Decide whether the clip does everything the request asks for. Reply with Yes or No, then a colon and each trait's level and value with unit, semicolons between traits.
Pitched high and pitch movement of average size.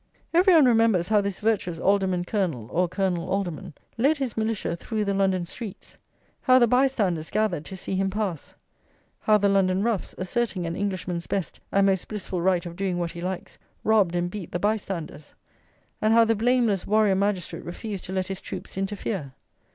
Yes: high, 195 Hz; average, 3.4 semitones